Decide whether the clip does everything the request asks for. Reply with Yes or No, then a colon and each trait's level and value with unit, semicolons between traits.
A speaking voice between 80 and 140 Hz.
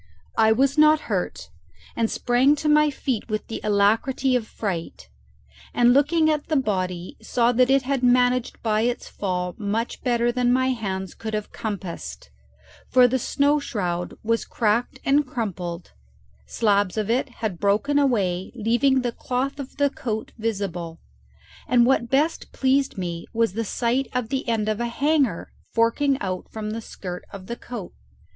No: high, 235 Hz